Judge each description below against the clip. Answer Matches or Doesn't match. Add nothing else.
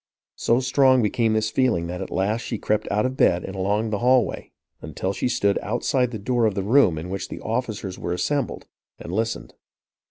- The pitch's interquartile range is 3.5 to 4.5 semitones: Matches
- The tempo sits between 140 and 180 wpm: Doesn't match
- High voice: Doesn't match